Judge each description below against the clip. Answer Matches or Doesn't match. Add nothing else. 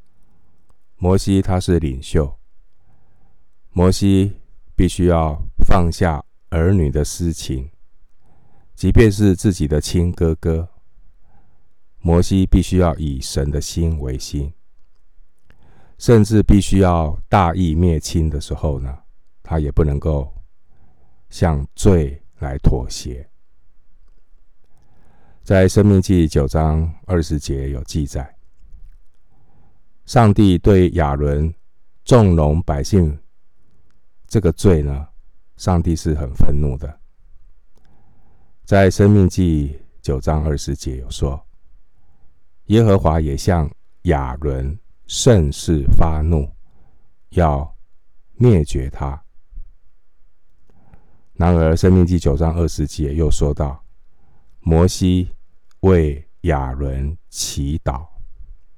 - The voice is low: Matches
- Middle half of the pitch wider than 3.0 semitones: Matches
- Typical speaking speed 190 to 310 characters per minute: Doesn't match